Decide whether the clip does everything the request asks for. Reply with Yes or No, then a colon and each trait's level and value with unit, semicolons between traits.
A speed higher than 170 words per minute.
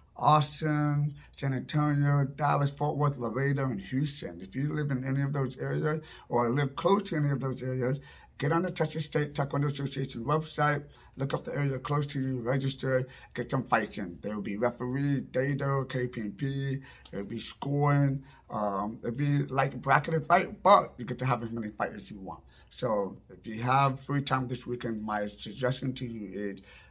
Yes: average, 195 wpm